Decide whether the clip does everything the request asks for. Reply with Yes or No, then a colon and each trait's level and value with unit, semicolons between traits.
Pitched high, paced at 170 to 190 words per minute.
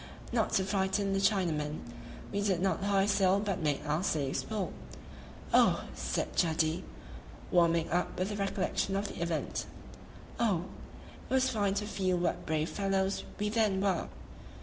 No: high, 195 Hz; average, 155 wpm